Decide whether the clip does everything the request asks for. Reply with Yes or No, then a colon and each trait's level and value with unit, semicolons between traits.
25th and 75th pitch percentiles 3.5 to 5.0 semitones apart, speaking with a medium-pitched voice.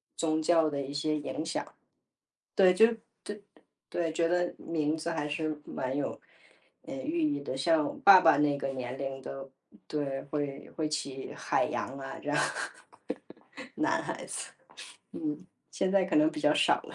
Yes: average, 4.1 semitones; medium, 155 Hz